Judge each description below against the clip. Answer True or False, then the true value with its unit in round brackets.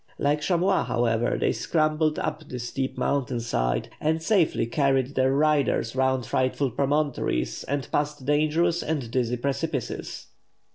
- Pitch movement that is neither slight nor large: True (3.5 semitones)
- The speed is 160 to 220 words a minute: False (135 wpm)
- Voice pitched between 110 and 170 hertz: True (140 Hz)